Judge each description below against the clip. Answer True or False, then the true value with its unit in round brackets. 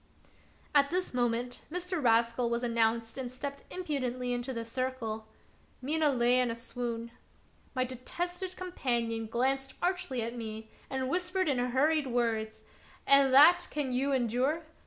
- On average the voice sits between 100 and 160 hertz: False (255 Hz)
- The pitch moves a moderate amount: True (3.5 semitones)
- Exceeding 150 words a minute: False (145 wpm)